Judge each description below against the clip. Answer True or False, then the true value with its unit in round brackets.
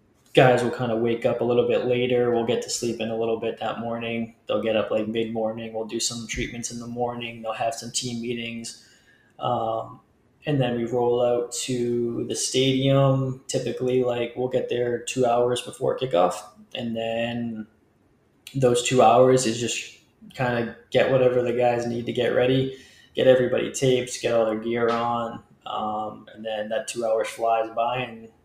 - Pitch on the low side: True (120 Hz)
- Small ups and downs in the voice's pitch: True (1.5 semitones)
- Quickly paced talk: False (190 wpm)